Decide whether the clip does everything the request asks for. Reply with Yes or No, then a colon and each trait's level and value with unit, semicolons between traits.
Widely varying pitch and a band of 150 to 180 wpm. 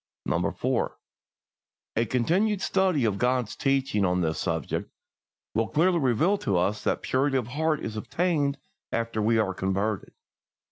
No: wide, 6.3 semitones; average, 140 wpm